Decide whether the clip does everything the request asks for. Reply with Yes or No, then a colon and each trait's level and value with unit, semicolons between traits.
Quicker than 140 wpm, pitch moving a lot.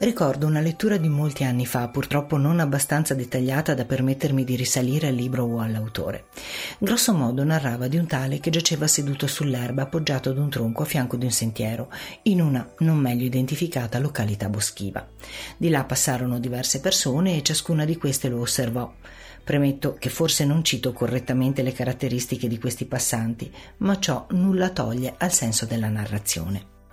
No: average, 165 wpm; average, 3.8 semitones